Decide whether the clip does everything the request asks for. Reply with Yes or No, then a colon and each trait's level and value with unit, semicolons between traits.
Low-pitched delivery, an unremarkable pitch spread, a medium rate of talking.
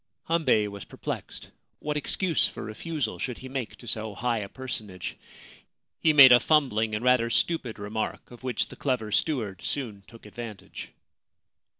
Yes: low, 120 Hz; average, 3.9 semitones; average, 160 wpm